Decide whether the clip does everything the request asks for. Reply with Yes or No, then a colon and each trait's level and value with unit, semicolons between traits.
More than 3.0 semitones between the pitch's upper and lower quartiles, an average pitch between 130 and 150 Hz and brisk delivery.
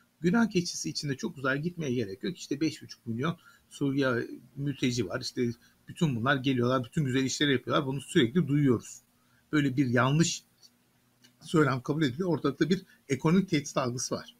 Yes: average, 4.0 semitones; medium, 140 Hz; fast, 155 wpm